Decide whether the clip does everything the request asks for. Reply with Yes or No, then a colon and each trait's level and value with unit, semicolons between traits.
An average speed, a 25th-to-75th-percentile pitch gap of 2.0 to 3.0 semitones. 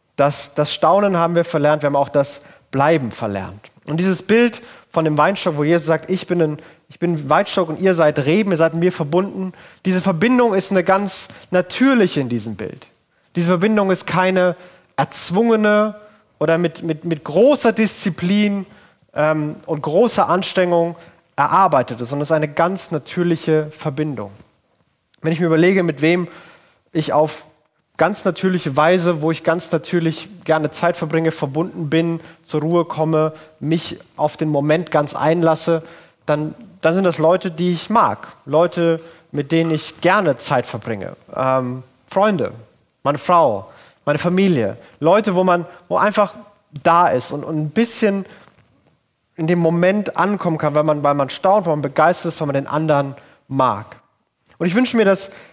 No: average, 165 wpm; average, 3.4 semitones